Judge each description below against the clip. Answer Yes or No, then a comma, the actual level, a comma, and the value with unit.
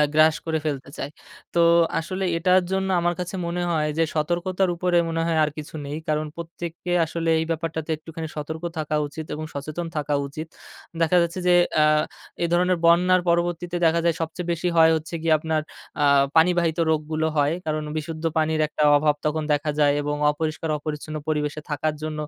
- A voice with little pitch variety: Yes, narrow, 1.9 semitones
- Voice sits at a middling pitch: Yes, medium, 160 Hz